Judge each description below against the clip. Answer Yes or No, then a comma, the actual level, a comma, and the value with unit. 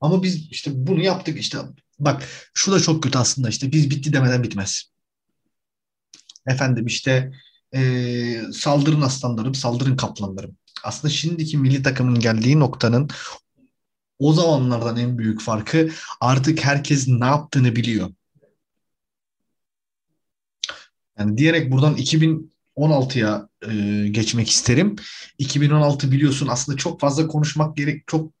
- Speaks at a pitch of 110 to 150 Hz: Yes, low, 135 Hz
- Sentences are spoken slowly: No, average, 115 wpm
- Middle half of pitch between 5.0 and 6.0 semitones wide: No, average, 3.9 semitones